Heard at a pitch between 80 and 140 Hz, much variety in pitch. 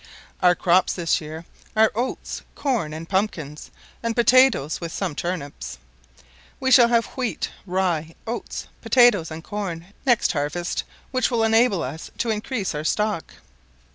No: high, 190 Hz; wide, 6.1 semitones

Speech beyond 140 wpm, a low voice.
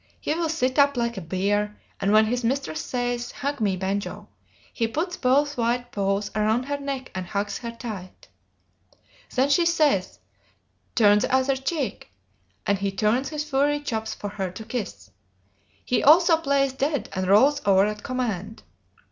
No: average, 165 wpm; high, 240 Hz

